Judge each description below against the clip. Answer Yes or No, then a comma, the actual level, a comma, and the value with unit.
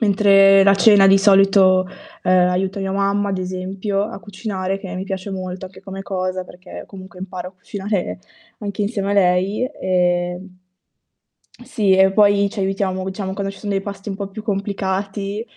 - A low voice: No, high, 195 Hz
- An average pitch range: No, narrow, 1.3 semitones